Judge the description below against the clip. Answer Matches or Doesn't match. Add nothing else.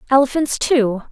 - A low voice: Doesn't match